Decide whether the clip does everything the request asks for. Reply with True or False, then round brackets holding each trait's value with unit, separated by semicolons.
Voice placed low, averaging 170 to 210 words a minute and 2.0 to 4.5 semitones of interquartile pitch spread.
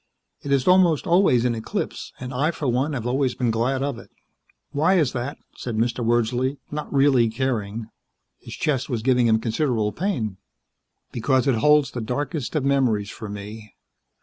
True (125 Hz; 175 wpm; 3.8 semitones)